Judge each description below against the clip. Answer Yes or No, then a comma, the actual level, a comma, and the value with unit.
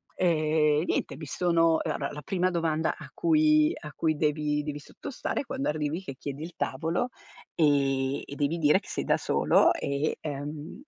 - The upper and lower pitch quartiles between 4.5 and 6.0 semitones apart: No, narrow, 2.6 semitones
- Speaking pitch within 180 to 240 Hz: No, medium, 155 Hz